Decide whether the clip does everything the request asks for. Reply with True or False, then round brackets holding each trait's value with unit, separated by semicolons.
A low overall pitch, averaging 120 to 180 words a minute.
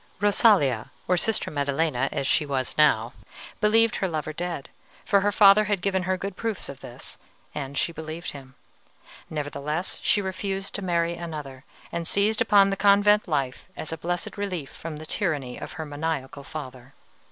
False (165 Hz; 170 wpm)